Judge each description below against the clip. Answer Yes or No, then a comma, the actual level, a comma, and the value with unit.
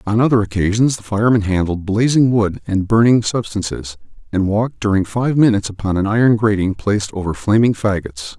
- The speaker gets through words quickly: No, average, 170 wpm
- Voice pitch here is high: No, low, 105 Hz